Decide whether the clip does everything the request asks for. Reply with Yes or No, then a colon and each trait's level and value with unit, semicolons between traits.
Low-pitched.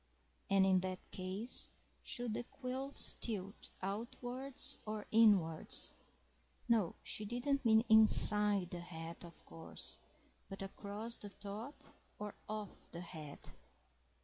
No: high, 210 Hz